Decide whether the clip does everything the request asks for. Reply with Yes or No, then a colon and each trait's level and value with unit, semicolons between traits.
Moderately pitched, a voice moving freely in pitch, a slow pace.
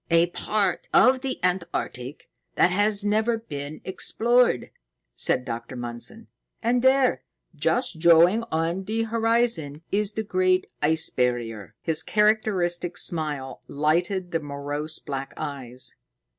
Yes: medium, 175 Hz; wide, 6.8 semitones; slow, 120 wpm